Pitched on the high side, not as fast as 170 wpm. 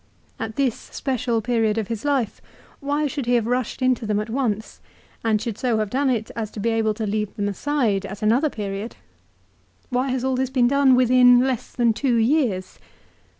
No: high, 235 Hz; average, 195 wpm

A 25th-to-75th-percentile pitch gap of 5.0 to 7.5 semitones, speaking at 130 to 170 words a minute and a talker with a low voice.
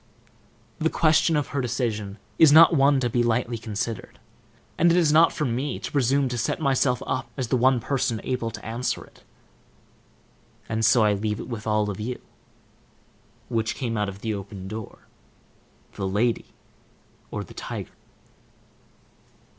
No: average, 3.9 semitones; average, 160 wpm; low, 120 Hz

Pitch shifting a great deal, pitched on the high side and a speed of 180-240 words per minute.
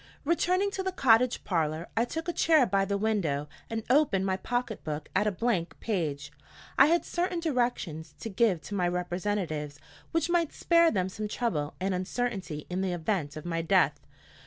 Yes: wide, 6.6 semitones; high, 200 Hz; average, 185 wpm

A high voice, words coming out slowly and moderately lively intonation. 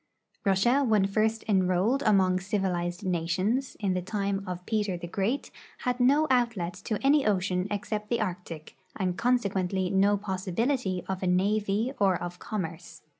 No: high, 195 Hz; average, 150 wpm; average, 3.2 semitones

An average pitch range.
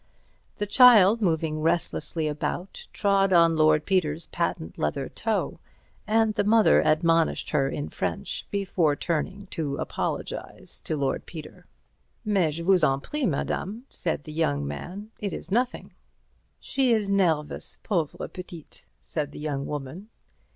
Yes: average, 4.8 semitones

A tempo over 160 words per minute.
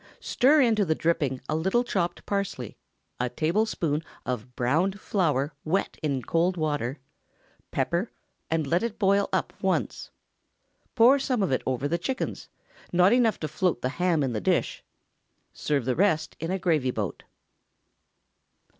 No: average, 145 wpm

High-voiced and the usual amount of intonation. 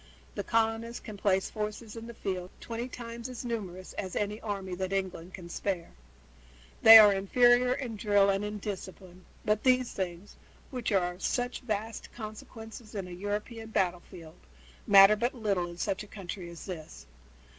Yes: high, 205 Hz; average, 3.3 semitones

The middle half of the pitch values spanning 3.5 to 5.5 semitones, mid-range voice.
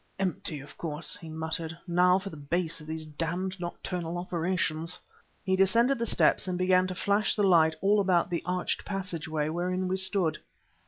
No: average, 2.7 semitones; medium, 180 Hz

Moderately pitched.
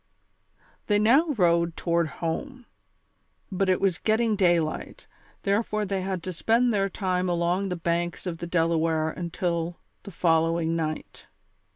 Yes: medium, 180 Hz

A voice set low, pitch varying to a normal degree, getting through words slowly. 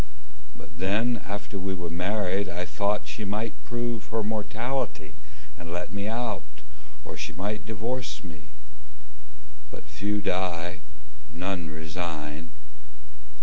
Yes: low, 100 Hz; average, 3.8 semitones; slow, 120 wpm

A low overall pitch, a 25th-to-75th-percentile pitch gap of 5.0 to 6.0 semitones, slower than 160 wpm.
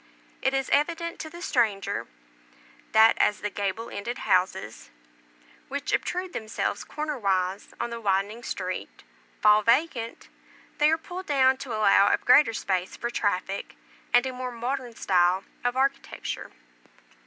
No: high, 235 Hz; average, 5.3 semitones; average, 145 wpm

